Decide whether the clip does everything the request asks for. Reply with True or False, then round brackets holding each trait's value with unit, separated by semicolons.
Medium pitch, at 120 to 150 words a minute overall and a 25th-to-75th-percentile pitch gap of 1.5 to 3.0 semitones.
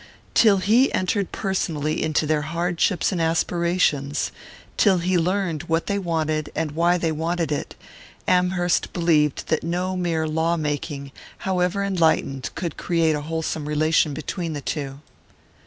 True (165 Hz; 140 wpm; 2.7 semitones)